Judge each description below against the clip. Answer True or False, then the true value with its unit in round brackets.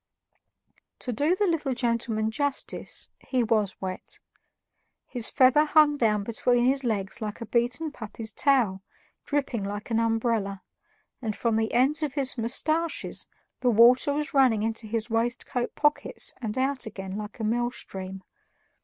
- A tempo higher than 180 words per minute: False (150 wpm)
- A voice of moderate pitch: False (235 Hz)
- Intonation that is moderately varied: True (3.8 semitones)